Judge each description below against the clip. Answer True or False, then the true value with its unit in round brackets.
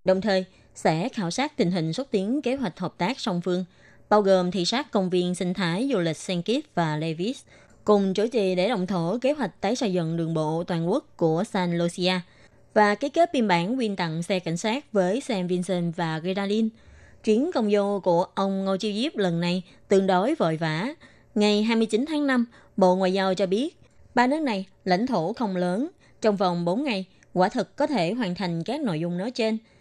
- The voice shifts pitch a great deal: False (4.3 semitones)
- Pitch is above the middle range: True (195 Hz)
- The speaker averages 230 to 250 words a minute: False (215 wpm)